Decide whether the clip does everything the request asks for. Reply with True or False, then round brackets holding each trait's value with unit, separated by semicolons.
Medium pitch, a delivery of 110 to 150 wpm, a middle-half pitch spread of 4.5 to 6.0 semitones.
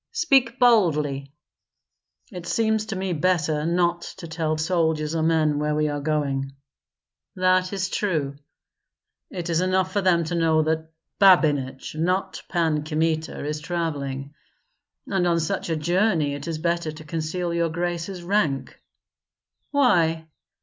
False (165 Hz; 140 wpm; 3.2 semitones)